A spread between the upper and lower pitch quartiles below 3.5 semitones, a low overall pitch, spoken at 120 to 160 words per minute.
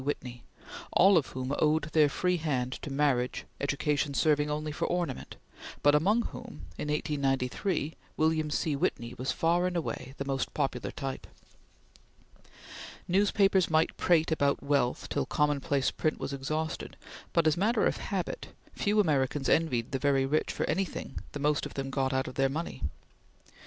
No: average, 3.1 semitones; medium, 150 Hz; average, 155 wpm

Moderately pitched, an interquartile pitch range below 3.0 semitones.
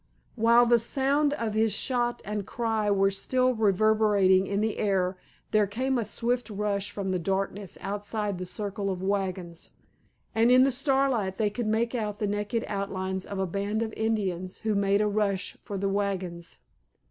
No: high, 205 Hz; narrow, 2.6 semitones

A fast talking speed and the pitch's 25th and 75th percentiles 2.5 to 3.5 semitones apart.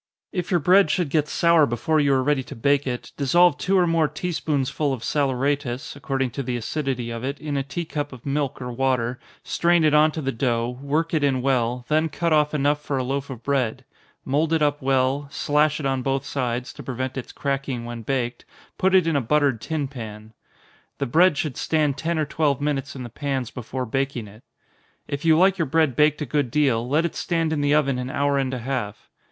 Yes: fast, 225 wpm; average, 3.1 semitones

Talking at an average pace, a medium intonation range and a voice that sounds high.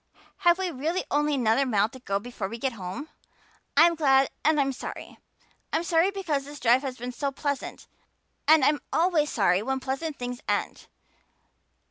Yes: average, 170 wpm; average, 4.3 semitones; very high, 275 Hz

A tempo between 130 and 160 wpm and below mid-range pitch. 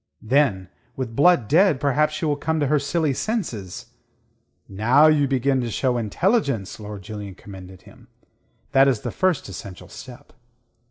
Yes: average, 155 wpm; low, 130 Hz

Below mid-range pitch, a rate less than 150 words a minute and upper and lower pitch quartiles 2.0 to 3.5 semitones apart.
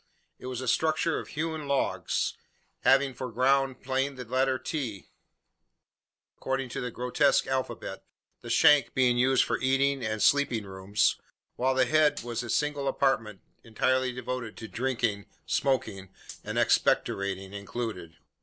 Yes: low, 130 Hz; average, 140 wpm; average, 3.2 semitones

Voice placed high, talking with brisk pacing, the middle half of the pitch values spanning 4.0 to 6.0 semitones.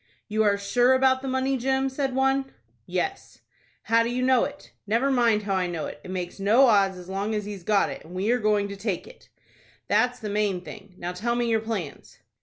Yes: high, 220 Hz; fast, 225 wpm; average, 4.7 semitones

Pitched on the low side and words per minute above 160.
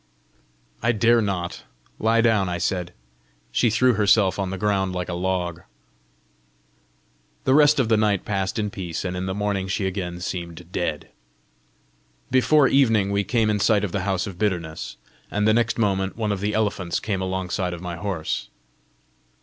Yes: low, 100 Hz; average, 175 wpm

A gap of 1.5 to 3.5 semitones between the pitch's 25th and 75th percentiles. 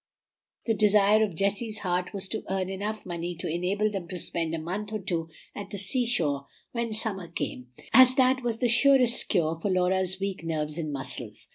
No: average, 4.0 semitones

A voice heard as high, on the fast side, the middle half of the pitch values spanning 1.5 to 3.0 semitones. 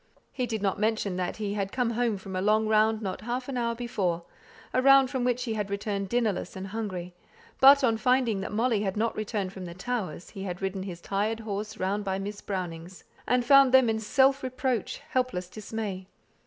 No: high, 215 Hz; fast, 210 wpm; average, 4.0 semitones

